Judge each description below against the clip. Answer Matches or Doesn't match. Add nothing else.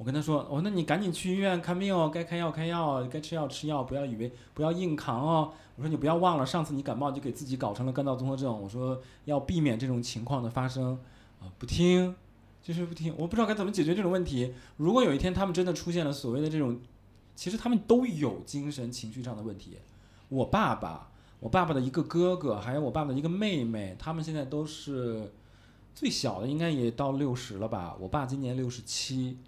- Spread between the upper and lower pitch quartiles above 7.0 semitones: Doesn't match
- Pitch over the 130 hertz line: Matches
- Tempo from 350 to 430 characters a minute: Matches